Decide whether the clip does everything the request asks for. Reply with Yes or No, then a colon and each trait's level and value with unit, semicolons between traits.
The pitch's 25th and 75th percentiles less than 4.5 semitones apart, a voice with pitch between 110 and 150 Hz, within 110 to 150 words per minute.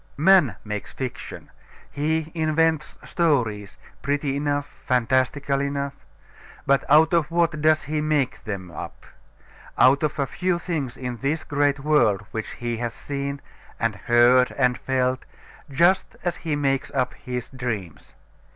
Yes: average, 3.5 semitones; medium, 140 Hz; average, 140 wpm